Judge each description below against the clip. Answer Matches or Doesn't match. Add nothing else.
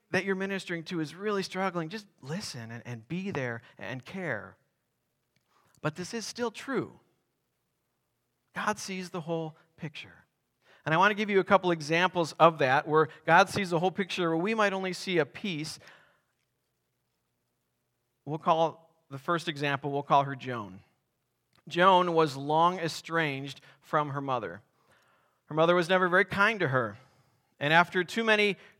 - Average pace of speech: Matches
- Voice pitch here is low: Doesn't match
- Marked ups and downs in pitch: Doesn't match